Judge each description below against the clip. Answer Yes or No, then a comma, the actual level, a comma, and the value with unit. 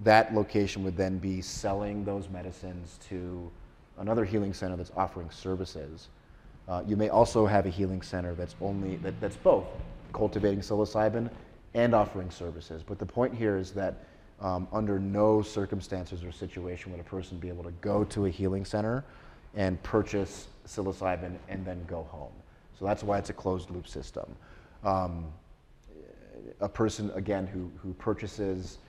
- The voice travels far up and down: No, narrow, 2.6 semitones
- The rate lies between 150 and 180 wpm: Yes, average, 160 wpm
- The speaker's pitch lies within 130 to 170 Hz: No, very low, 95 Hz